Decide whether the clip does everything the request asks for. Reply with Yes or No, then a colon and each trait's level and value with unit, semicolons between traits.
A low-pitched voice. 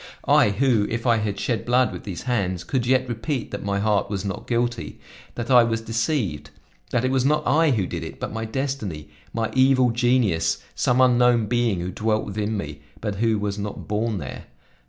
Yes: low, 115 Hz